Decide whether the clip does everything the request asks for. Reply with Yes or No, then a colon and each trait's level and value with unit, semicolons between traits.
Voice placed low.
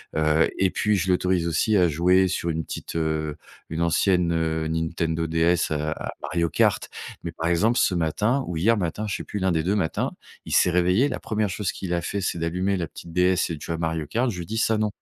Yes: very low, 85 Hz